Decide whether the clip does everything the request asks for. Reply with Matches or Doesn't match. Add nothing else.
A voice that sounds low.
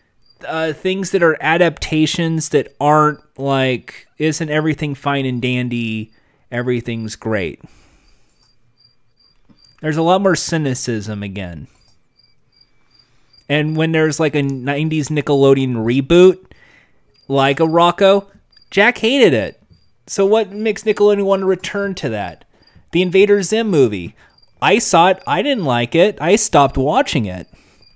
Doesn't match